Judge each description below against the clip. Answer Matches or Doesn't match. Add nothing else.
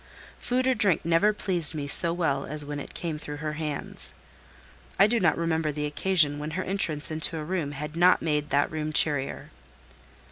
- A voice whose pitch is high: Doesn't match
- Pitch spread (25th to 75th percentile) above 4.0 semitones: Doesn't match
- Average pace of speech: Matches